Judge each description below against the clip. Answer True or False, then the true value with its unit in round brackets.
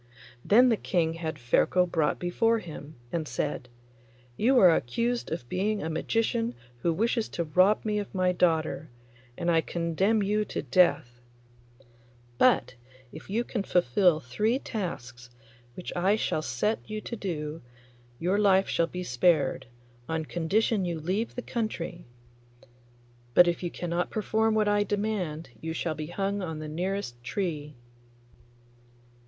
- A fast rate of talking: False (150 wpm)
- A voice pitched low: False (180 Hz)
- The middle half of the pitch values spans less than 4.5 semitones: False (4.8 semitones)